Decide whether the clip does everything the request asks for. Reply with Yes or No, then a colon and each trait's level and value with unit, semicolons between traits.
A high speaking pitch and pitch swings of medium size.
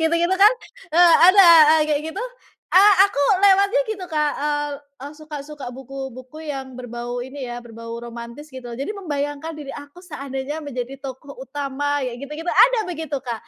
Yes: very high, 285 Hz; average, 3.7 semitones